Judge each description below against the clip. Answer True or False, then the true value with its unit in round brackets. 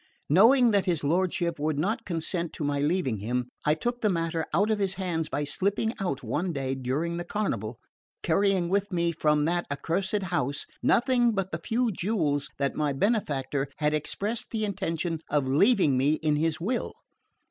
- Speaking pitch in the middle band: True (170 Hz)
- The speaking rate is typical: True (180 wpm)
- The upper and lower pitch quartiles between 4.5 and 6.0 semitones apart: True (5.2 semitones)